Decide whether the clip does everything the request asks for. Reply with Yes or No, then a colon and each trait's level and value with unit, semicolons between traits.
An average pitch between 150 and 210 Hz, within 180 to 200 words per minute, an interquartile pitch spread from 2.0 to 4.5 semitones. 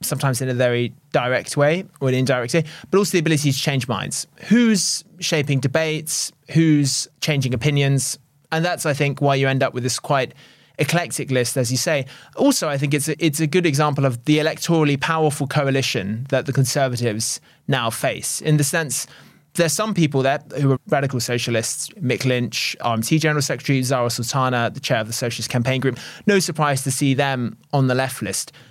No: medium, 140 Hz; average, 190 wpm; average, 3.5 semitones